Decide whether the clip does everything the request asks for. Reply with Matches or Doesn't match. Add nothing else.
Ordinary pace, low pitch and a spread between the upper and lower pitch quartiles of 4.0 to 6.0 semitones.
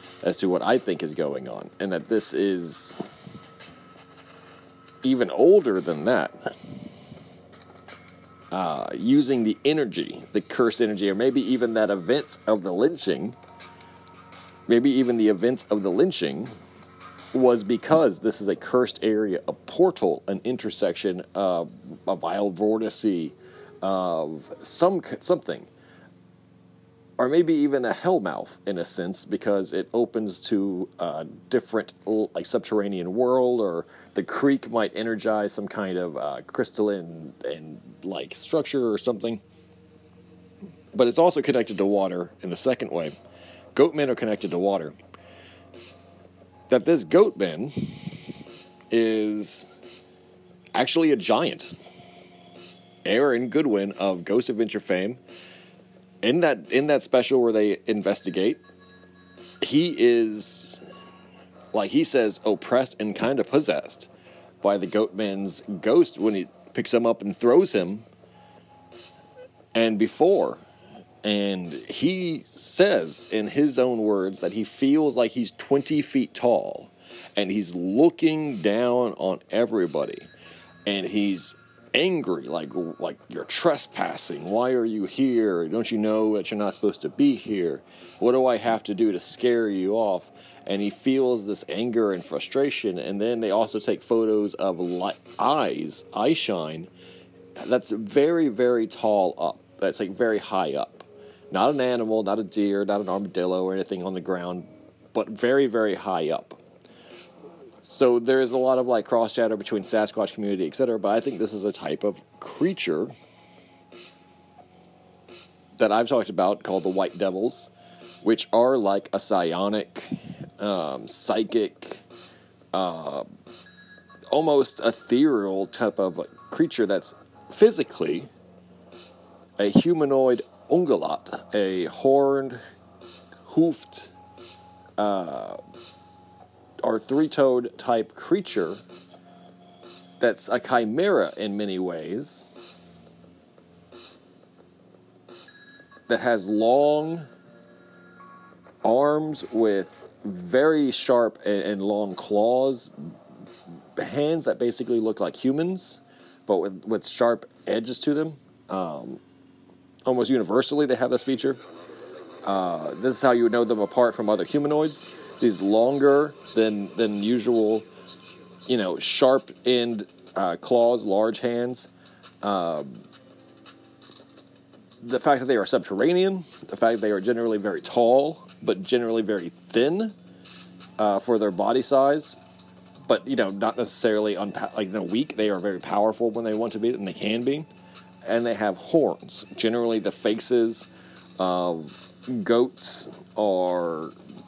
Doesn't match